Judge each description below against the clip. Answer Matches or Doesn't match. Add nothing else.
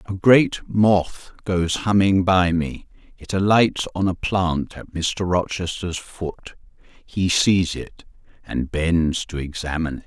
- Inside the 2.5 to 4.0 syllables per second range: Matches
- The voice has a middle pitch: Doesn't match